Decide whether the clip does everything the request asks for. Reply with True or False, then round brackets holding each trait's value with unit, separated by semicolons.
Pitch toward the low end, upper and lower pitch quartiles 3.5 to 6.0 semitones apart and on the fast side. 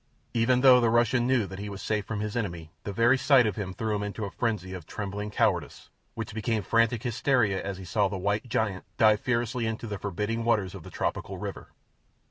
False (110 Hz; 2.9 semitones; 220 wpm)